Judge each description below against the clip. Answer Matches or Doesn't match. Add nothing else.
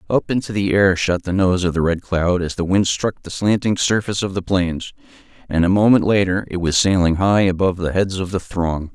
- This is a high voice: Doesn't match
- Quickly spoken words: Matches